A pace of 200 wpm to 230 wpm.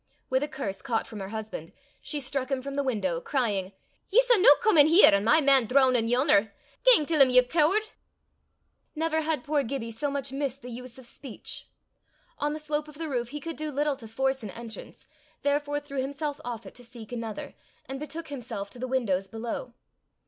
Yes: fast, 205 wpm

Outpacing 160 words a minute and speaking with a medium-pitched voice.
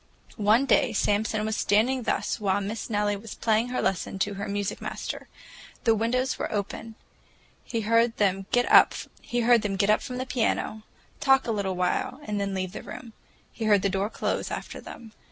No: average, 175 wpm; high, 215 Hz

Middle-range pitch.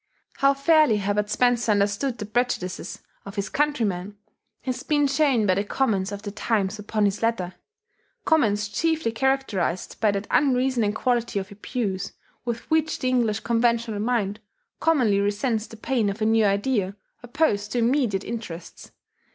No: high, 225 Hz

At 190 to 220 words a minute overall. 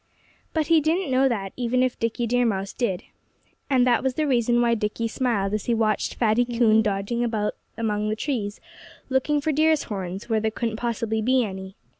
Yes: average, 195 wpm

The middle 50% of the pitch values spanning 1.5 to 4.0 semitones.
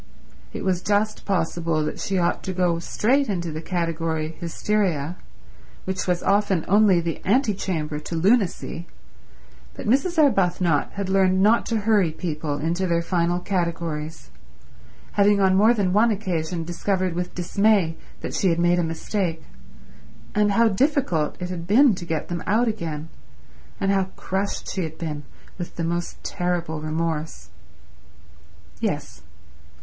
Yes: average, 3.5 semitones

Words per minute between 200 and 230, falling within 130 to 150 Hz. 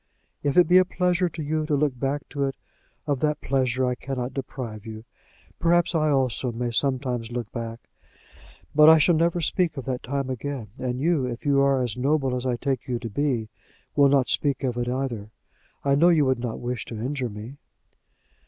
Yes: fast, 205 wpm; low, 135 Hz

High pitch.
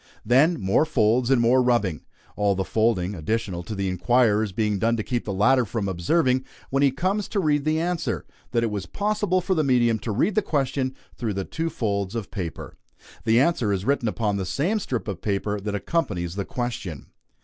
No: low, 115 Hz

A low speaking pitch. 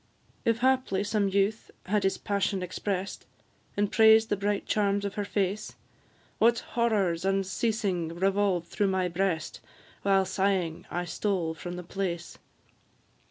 No: high, 195 Hz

